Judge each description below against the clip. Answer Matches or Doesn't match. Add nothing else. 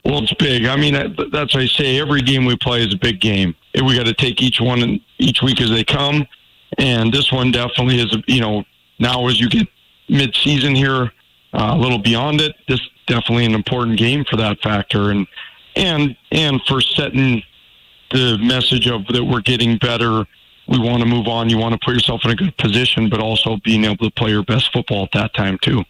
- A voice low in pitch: Matches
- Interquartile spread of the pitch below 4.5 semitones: Matches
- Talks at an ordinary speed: Doesn't match